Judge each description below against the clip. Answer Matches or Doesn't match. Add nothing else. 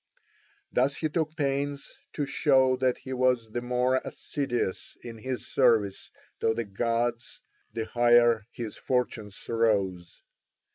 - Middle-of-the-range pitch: Doesn't match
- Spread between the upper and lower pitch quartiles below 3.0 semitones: Matches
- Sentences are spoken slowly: Matches